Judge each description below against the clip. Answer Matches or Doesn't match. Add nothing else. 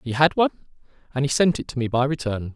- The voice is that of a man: Matches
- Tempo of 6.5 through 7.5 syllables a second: Matches